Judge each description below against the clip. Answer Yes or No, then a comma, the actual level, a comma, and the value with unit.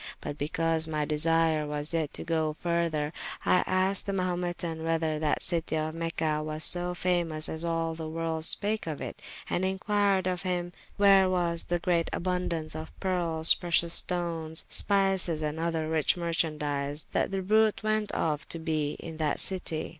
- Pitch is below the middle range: No, medium, 165 Hz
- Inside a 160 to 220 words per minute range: Yes, average, 170 wpm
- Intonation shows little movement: Yes, narrow, 2.3 semitones